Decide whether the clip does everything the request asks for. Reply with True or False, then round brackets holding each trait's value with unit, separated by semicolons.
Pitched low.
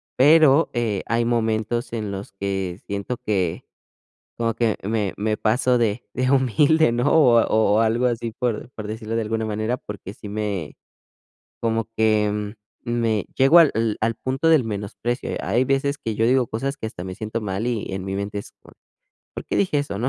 True (115 Hz)